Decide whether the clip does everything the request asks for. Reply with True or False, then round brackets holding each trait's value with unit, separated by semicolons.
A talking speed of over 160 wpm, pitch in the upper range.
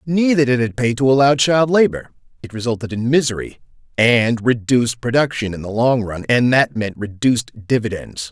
False (175 wpm; 120 Hz)